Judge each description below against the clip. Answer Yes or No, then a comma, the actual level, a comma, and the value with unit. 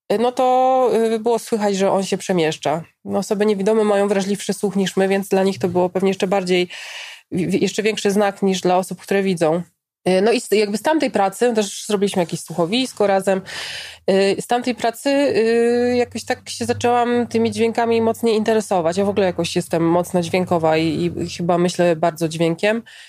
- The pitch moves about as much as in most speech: Yes, average, 3.9 semitones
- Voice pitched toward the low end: No, high, 200 Hz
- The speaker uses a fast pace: Yes, fast, 170 wpm